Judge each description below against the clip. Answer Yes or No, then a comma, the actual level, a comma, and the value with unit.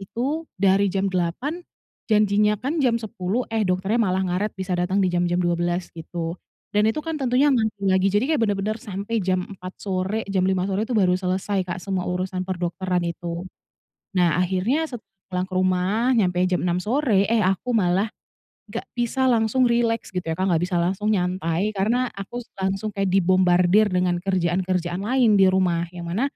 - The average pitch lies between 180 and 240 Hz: Yes, high, 190 Hz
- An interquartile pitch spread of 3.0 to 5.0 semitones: Yes, average, 3.3 semitones